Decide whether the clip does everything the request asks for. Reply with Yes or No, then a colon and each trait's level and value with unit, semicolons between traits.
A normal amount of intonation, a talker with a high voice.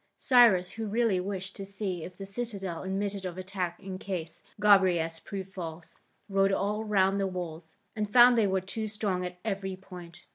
No: narrow, 2.0 semitones; high, 195 Hz